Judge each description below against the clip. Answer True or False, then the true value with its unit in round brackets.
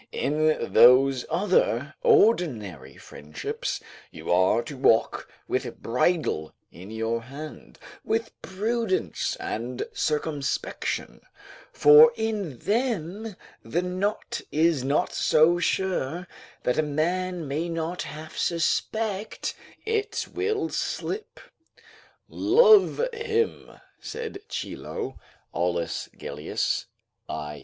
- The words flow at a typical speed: False (95 wpm)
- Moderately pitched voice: True (165 Hz)